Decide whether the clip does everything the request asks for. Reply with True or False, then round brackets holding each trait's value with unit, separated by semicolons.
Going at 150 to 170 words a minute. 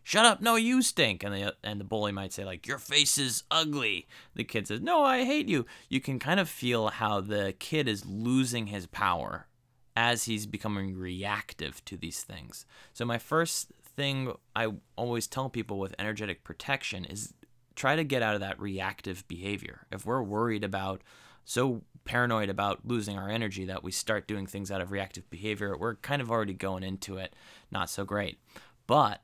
False (190 wpm)